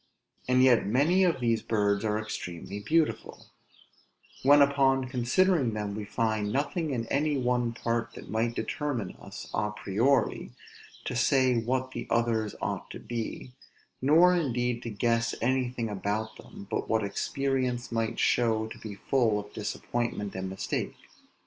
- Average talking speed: Yes, average, 150 wpm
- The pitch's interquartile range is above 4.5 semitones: No, average, 3.4 semitones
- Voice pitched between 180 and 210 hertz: No, low, 120 Hz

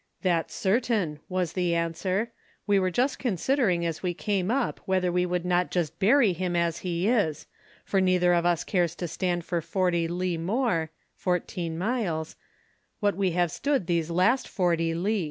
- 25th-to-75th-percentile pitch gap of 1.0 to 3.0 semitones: Yes, narrow, 2.6 semitones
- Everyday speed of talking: Yes, average, 175 wpm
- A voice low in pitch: No, medium, 180 Hz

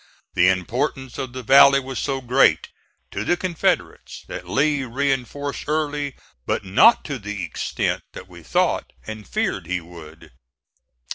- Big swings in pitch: Yes, wide, 6.2 semitones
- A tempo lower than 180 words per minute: Yes, average, 145 wpm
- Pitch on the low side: Yes, low, 130 Hz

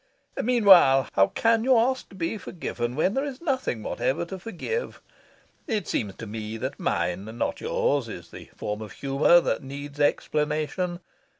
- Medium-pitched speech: Yes, medium, 150 Hz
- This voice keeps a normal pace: Yes, average, 165 wpm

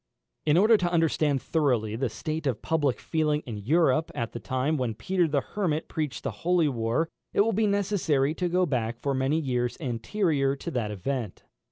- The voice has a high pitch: No, medium, 145 Hz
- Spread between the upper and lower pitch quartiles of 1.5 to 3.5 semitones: No, average, 5.1 semitones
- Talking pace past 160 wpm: Yes, average, 190 wpm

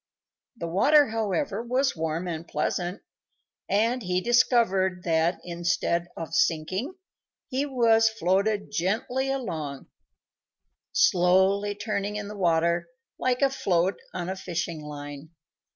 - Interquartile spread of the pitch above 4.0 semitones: Yes, average, 4.9 semitones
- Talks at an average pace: No, slow, 120 wpm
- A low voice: No, high, 190 Hz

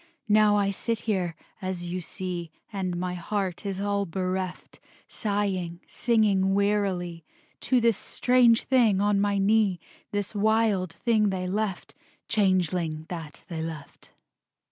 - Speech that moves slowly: Yes, slow, 130 wpm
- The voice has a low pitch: No, high, 195 Hz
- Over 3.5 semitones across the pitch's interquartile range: No, narrow, 2.6 semitones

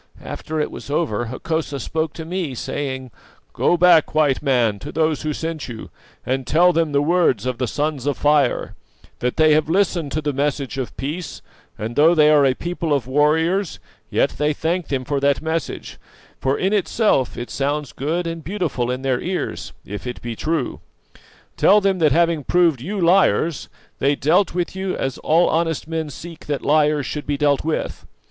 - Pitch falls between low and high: Yes, medium, 150 Hz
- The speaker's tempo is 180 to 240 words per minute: Yes, average, 190 wpm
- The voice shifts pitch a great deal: No, average, 3.6 semitones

